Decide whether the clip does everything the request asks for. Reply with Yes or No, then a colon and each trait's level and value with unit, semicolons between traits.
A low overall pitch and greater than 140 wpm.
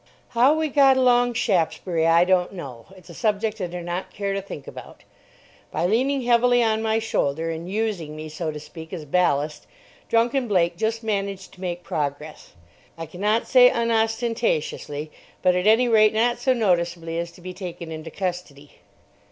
No: medium, 185 Hz; average, 175 wpm